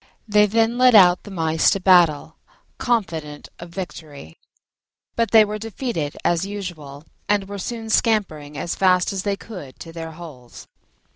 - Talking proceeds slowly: No, average, 155 wpm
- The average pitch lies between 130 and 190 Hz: Yes, medium, 185 Hz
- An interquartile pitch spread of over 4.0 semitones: Yes, average, 4.8 semitones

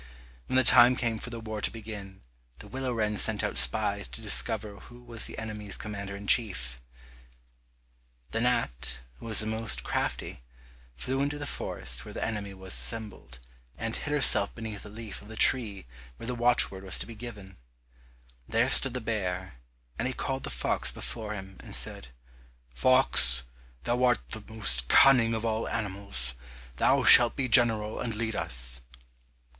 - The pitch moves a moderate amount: Yes, average, 3.7 semitones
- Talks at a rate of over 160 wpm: Yes, average, 170 wpm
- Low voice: Yes, low, 110 Hz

